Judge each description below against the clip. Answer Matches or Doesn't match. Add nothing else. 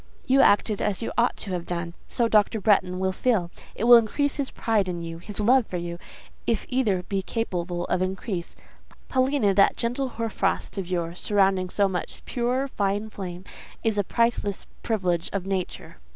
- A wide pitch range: Doesn't match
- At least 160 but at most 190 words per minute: Matches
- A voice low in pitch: Doesn't match